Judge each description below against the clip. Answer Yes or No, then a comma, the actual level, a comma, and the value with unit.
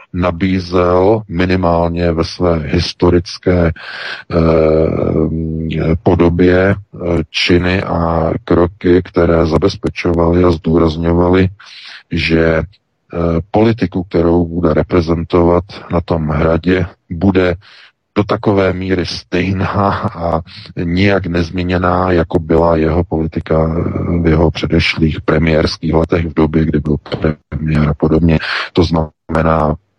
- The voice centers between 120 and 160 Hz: No, very low, 85 Hz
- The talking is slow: Yes, slow, 100 wpm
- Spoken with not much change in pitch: Yes, narrow, 2.1 semitones